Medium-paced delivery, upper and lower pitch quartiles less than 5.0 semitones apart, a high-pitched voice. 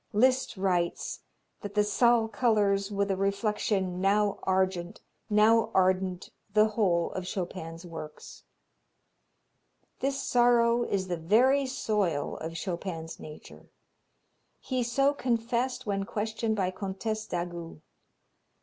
No: slow, 115 wpm; average, 3.7 semitones; high, 200 Hz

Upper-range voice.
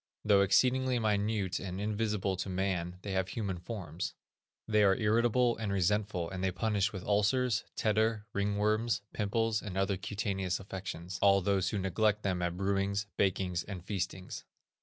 No: low, 100 Hz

